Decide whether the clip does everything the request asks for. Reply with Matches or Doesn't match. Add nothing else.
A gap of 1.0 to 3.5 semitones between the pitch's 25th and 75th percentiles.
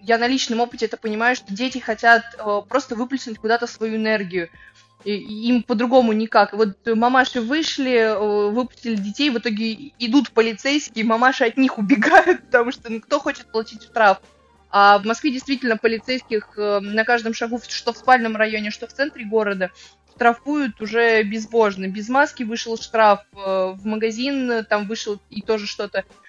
Matches